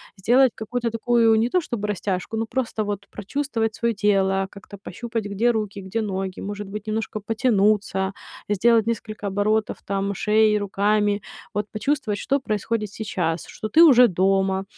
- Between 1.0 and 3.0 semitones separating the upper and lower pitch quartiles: Yes, narrow, 2.4 semitones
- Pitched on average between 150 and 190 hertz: No, high, 210 Hz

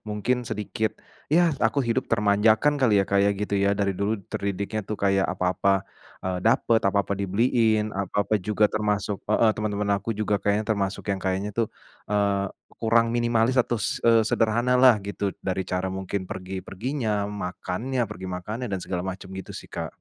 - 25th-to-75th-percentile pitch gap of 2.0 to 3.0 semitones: Yes, narrow, 2.4 semitones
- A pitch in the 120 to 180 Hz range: No, low, 105 Hz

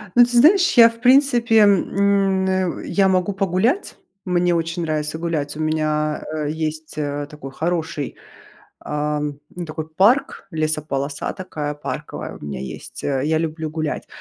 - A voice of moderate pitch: Yes, medium, 160 Hz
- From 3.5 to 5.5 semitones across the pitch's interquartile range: Yes, average, 4.2 semitones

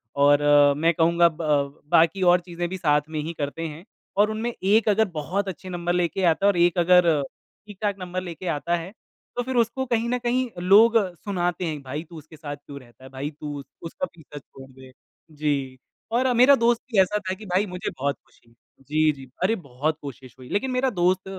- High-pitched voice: No, medium, 170 Hz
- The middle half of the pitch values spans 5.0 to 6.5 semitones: Yes, wide, 5.4 semitones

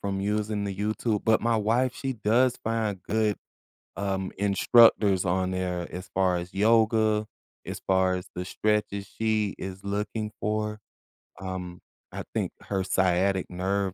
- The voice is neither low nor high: No, low, 100 Hz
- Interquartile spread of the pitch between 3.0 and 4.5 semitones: No, narrow, 2.4 semitones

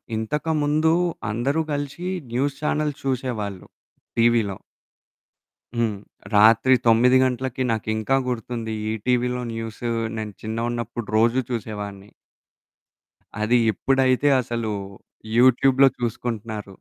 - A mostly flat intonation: No, average, 3.0 semitones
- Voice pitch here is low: Yes, low, 120 Hz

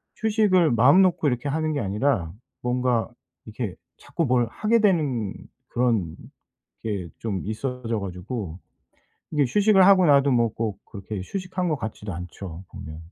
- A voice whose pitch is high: No, low, 125 Hz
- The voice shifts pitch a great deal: Yes, wide, 7.3 semitones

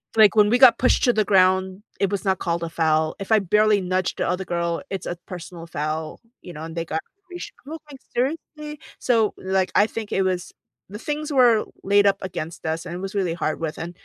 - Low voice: No, high, 190 Hz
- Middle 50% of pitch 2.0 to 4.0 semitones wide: No, average, 4.4 semitones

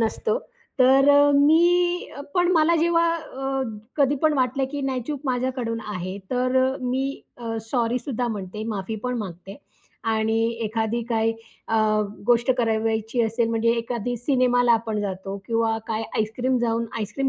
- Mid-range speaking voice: No, high, 240 Hz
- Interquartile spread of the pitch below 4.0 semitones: Yes, average, 3.3 semitones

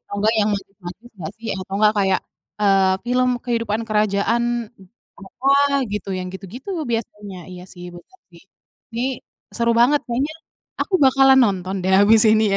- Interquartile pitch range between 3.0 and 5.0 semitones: Yes, average, 3.7 semitones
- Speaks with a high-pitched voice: Yes, high, 210 Hz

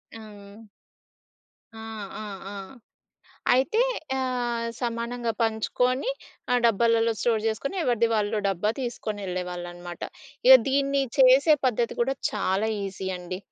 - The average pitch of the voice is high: Yes, high, 230 Hz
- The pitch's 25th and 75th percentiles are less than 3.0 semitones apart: No, average, 3.5 semitones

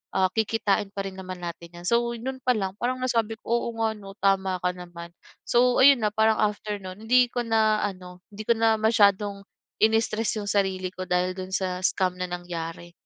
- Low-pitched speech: No, high, 200 Hz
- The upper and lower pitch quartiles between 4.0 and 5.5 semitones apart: No, average, 3.3 semitones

